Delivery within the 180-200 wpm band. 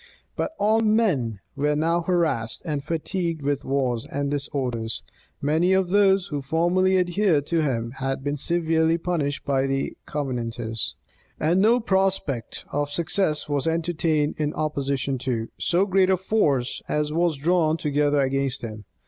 No: average, 150 wpm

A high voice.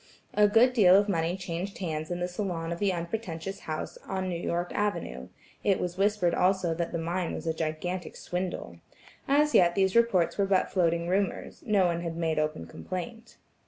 No: medium, 180 Hz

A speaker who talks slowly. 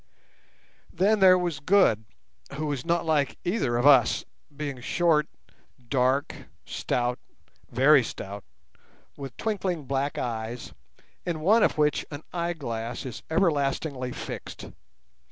Yes: slow, 110 wpm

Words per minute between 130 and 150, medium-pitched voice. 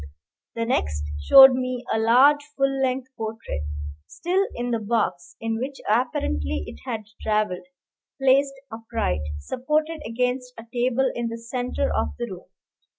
No: average, 145 wpm; high, 240 Hz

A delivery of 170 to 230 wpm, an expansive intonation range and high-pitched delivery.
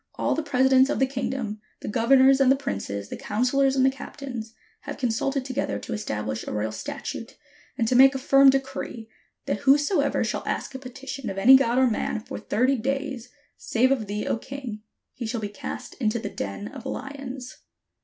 No: average, 200 wpm; average, 3.6 semitones; very high, 255 Hz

